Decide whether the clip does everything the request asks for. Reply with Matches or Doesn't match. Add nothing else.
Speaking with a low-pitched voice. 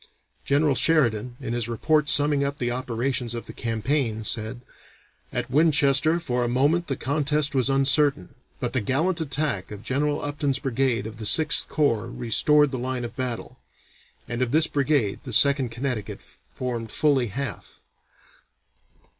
Matches